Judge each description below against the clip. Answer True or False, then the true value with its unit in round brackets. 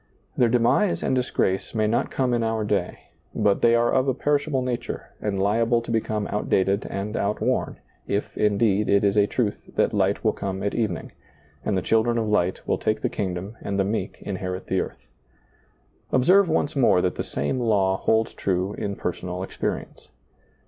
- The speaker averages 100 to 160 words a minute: False (185 wpm)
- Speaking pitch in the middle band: False (105 Hz)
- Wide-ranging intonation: False (3.3 semitones)